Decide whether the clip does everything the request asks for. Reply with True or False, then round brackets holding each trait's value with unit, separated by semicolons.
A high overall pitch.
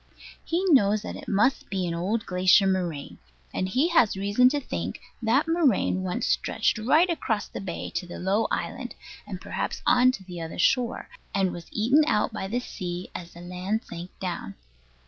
True (200 Hz)